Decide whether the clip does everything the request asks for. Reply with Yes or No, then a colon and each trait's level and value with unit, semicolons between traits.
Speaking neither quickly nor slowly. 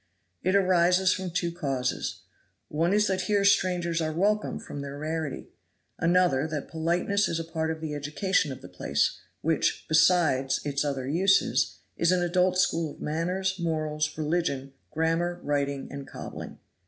Yes: average, 155 wpm